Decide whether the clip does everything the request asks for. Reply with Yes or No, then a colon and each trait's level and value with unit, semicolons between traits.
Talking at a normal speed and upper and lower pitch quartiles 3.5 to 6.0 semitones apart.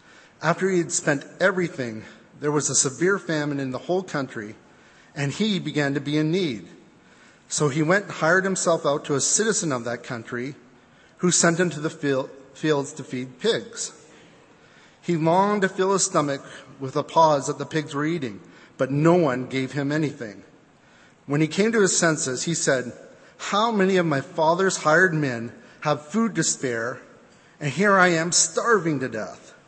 Yes: average, 180 wpm; average, 4.3 semitones